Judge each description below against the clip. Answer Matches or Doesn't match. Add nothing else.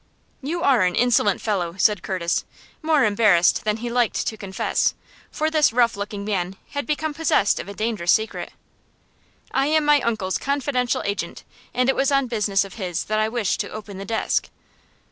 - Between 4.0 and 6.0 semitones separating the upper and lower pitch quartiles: Matches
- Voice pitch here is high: Matches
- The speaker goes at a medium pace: Matches